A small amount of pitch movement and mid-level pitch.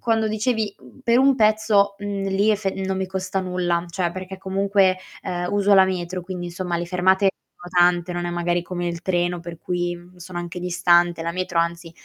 Yes: narrow, 1.9 semitones; medium, 180 Hz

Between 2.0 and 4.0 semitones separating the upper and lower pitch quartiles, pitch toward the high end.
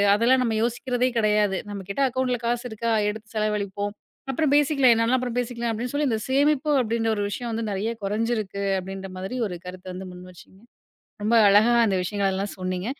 Yes: average, 3.6 semitones; high, 220 Hz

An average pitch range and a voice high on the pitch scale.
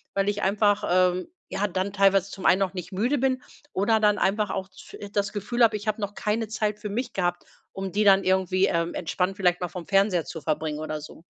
No: narrow, 2.3 semitones; high, 195 Hz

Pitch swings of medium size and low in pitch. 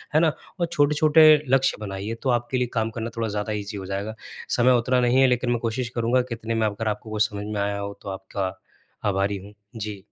Yes: average, 3.5 semitones; low, 115 Hz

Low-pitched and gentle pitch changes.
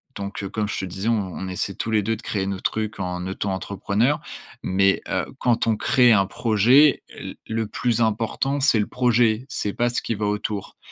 No: low, 110 Hz; average, 3.0 semitones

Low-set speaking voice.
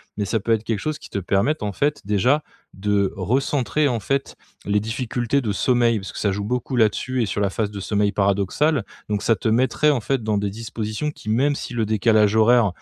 Yes: low, 110 Hz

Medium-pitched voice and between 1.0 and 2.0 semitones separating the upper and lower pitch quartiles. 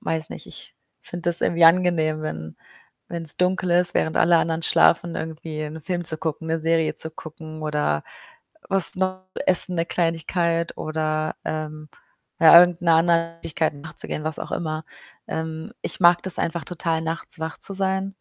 Yes: medium, 165 Hz; narrow, 1.7 semitones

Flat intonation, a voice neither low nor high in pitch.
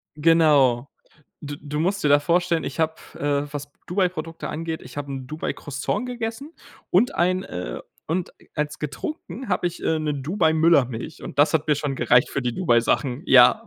No: average, 3.8 semitones; medium, 150 Hz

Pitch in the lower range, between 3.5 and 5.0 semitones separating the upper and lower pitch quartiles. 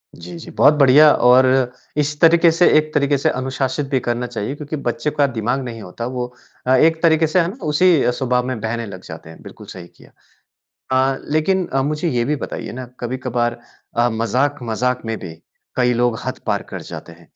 Yes: low, 130 Hz; average, 4.0 semitones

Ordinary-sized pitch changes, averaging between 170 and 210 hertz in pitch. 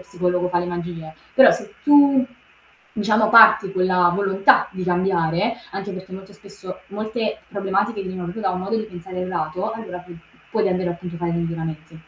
Yes: average, 3.0 semitones; medium, 185 Hz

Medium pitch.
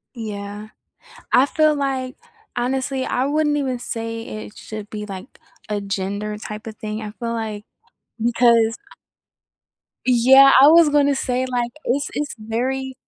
No: high, 240 Hz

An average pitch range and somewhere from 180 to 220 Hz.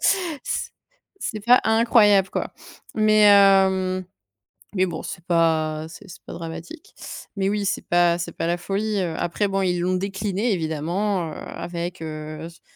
Yes: average, 3.4 semitones; medium, 185 Hz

